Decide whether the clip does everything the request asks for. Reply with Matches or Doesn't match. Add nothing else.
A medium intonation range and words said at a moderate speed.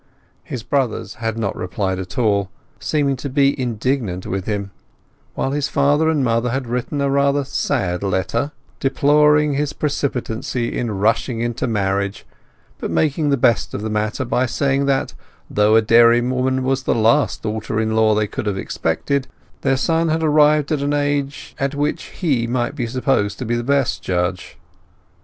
Matches